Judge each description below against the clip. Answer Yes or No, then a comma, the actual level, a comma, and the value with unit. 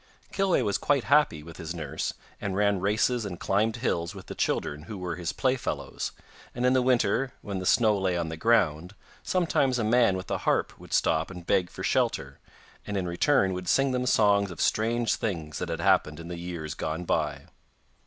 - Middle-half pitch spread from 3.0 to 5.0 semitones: No, wide, 5.6 semitones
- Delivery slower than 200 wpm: No, fast, 205 wpm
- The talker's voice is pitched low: Yes, low, 100 Hz